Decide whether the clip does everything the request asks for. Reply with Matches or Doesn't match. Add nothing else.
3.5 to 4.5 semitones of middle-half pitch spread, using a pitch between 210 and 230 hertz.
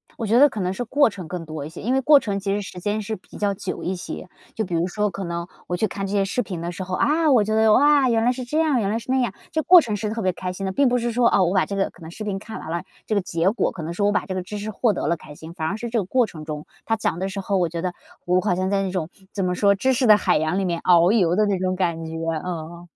Doesn't match